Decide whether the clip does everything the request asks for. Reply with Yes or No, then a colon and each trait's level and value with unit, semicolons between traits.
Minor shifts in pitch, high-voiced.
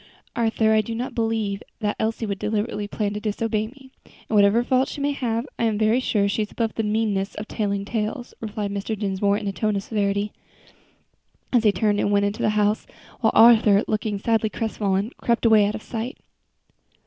Yes: narrow, 1.8 semitones; high, 215 Hz